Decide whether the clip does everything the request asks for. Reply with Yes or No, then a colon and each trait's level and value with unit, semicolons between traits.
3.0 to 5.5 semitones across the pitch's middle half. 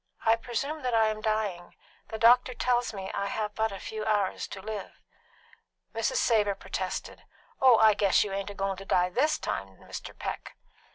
No: narrow, 2.5 semitones